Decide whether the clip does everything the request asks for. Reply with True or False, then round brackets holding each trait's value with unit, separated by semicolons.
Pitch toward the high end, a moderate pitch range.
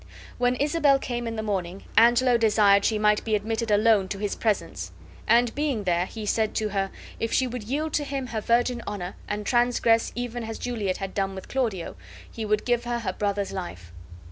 True (220 Hz; 3.1 semitones)